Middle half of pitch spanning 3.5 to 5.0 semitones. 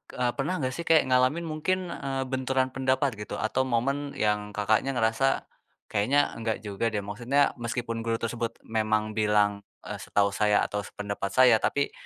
Yes: average, 4.0 semitones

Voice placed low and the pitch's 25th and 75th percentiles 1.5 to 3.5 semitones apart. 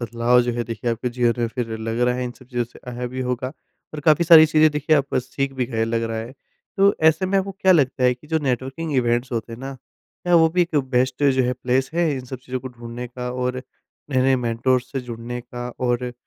Yes: low, 125 Hz; average, 2.7 semitones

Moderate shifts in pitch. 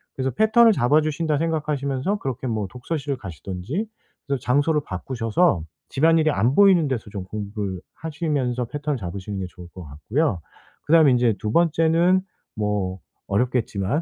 No: wide, 7.2 semitones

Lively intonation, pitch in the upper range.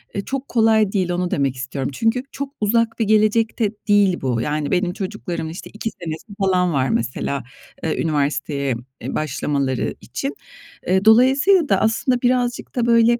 Yes: wide, 7.6 semitones; high, 195 Hz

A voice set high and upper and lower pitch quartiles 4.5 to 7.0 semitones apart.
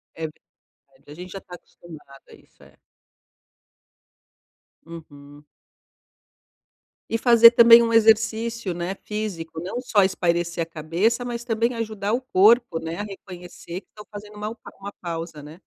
Yes: high, 195 Hz; average, 5.2 semitones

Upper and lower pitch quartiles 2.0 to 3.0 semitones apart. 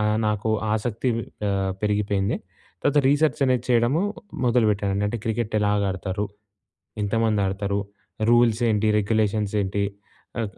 Yes: narrow, 2.5 semitones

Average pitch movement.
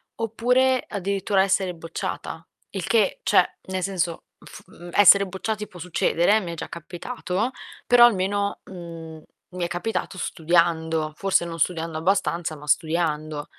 Yes: average, 3.3 semitones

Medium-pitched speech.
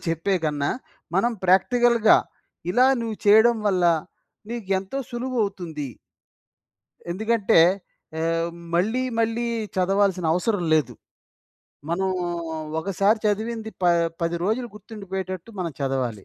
No: high, 195 Hz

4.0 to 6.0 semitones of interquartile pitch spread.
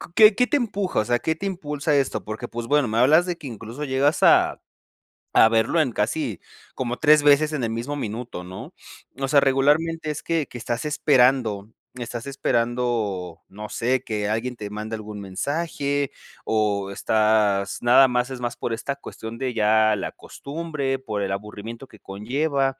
Yes: average, 5.0 semitones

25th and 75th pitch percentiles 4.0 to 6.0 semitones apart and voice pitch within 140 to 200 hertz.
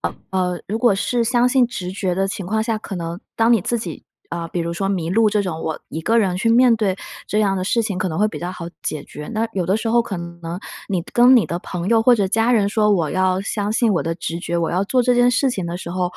Yes: average, 4.3 semitones; high, 195 Hz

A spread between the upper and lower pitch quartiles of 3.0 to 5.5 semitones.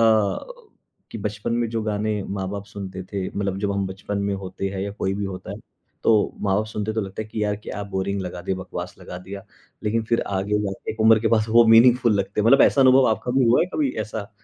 No: narrow, 2.4 semitones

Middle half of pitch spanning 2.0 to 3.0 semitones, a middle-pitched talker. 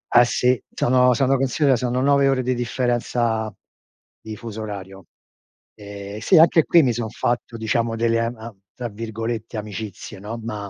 No: narrow, 2.6 semitones; low, 115 Hz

